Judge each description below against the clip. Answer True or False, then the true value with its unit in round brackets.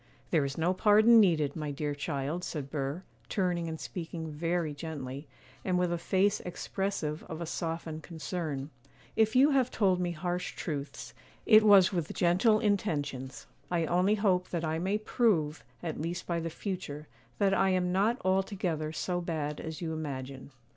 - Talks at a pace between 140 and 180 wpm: True (170 wpm)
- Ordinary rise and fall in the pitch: True (3.8 semitones)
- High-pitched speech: False (170 Hz)